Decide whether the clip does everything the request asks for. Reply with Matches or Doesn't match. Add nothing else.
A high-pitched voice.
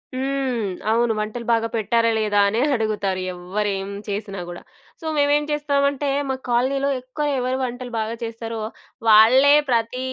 Matches